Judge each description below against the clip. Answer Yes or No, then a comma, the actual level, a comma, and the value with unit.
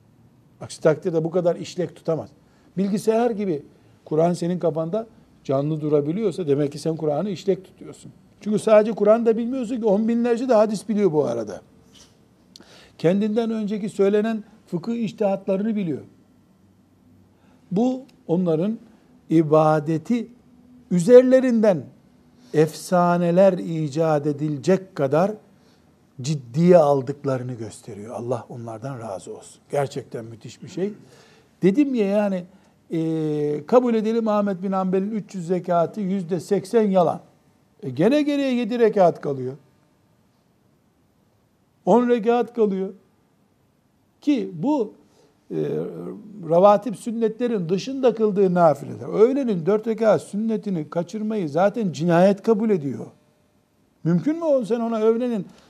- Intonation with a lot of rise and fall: Yes, wide, 5.8 semitones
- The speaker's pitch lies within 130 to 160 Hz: No, high, 190 Hz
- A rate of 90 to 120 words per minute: Yes, average, 110 wpm